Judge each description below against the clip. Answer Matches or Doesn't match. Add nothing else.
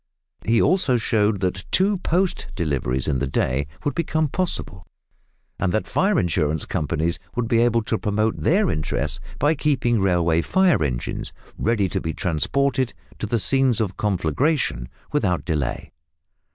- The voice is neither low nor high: Doesn't match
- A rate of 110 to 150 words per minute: Matches